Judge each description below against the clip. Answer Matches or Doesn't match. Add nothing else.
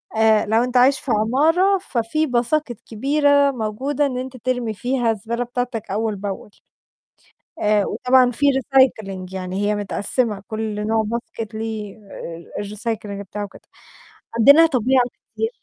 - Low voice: Doesn't match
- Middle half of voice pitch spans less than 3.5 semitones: Doesn't match